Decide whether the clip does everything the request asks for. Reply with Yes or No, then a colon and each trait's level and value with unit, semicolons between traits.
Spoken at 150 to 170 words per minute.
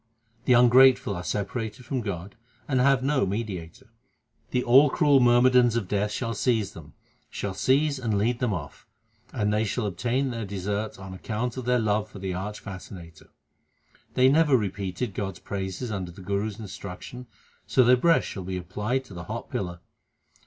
No: average, 180 wpm